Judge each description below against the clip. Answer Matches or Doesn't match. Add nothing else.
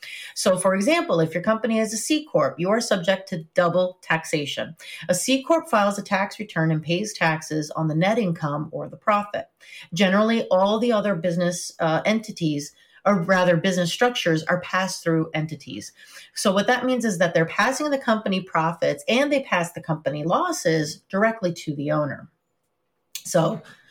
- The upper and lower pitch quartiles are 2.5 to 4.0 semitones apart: Doesn't match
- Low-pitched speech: Doesn't match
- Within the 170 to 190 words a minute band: Matches